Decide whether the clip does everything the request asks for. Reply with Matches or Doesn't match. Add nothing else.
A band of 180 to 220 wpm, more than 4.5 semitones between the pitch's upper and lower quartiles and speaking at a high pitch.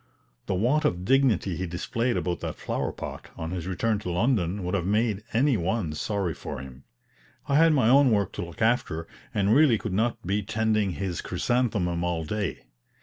Doesn't match